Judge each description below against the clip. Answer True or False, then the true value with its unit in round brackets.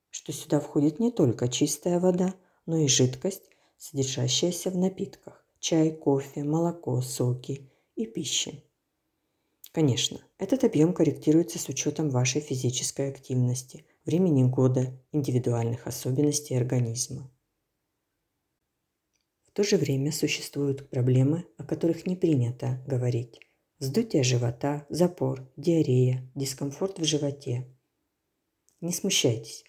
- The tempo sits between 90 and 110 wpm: True (105 wpm)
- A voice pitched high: False (145 Hz)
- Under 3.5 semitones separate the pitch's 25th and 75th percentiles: False (4.3 semitones)